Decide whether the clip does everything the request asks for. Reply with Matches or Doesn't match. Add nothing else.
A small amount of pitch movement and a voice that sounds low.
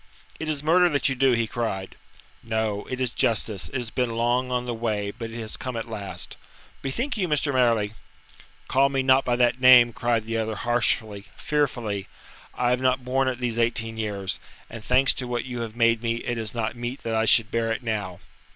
Matches